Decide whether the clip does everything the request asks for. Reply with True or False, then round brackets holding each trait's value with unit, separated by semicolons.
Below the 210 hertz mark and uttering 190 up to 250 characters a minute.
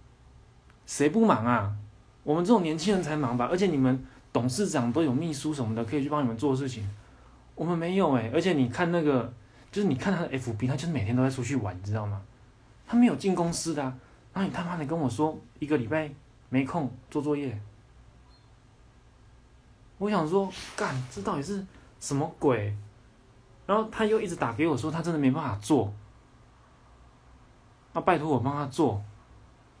False (135 Hz; 270 characters per minute)